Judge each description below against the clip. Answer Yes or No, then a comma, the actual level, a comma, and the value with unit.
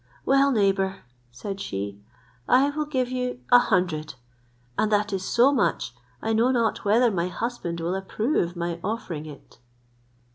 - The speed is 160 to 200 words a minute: No, average, 150 wpm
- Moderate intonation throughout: No, wide, 6.1 semitones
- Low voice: No, high, 205 Hz